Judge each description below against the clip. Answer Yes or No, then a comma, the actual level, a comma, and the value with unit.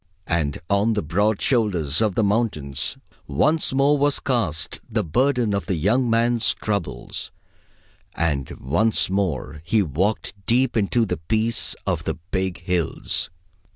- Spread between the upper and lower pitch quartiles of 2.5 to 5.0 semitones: No, wide, 5.6 semitones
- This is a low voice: Yes, low, 100 Hz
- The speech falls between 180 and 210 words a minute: No, average, 140 wpm